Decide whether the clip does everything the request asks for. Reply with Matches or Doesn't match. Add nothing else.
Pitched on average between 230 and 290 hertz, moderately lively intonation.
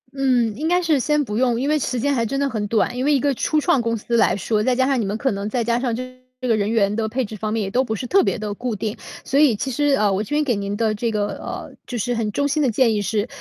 Matches